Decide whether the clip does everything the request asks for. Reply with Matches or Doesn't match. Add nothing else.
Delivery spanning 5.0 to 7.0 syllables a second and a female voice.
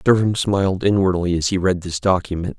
Doesn't match